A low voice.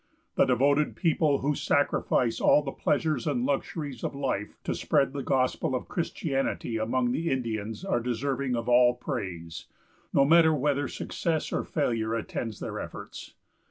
Yes: low, 130 Hz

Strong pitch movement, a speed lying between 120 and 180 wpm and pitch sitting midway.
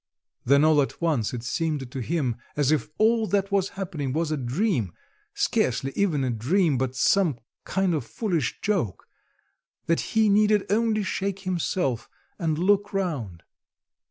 Yes: wide, 7.0 semitones; average, 155 wpm; medium, 165 Hz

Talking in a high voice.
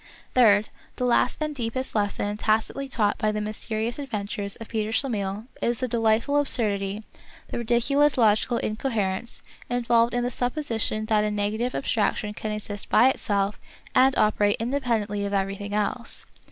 Yes: high, 220 Hz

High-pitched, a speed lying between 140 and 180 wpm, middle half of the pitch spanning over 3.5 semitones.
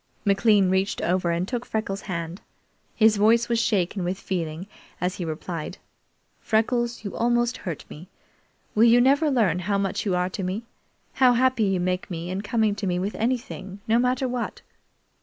Yes: high, 200 Hz; average, 175 wpm; average, 4.4 semitones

